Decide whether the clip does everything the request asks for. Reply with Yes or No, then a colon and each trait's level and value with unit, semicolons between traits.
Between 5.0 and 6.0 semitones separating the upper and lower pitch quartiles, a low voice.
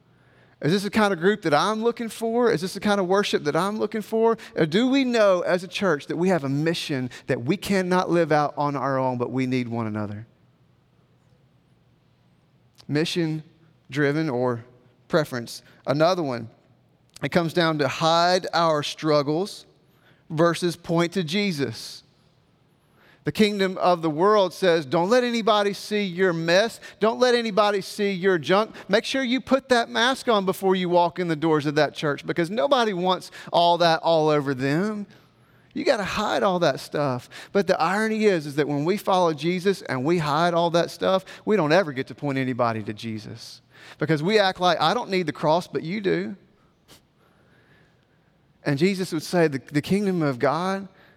No: average, 5.3 semitones; medium, 170 Hz